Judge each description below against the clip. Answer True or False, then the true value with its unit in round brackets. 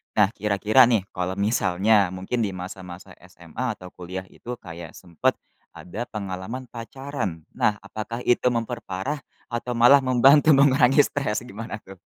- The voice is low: True (105 Hz)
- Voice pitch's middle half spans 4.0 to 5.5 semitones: True (4.8 semitones)